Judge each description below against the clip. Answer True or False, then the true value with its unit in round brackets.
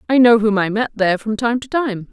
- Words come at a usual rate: False (285 wpm)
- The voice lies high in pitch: True (225 Hz)